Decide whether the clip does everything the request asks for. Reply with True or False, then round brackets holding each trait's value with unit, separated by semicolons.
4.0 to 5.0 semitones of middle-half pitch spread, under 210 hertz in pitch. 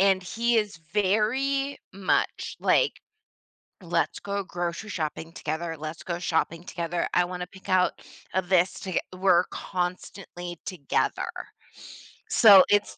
False (2.7 semitones; 185 Hz)